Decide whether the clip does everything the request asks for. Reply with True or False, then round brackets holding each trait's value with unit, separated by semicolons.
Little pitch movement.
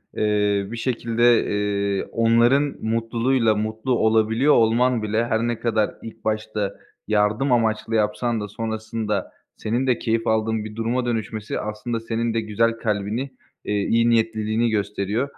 True (1.6 semitones)